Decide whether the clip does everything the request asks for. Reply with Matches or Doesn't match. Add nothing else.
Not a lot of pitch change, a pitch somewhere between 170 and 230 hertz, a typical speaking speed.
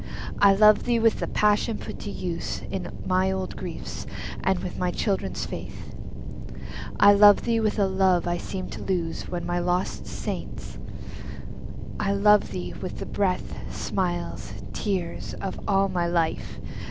Matches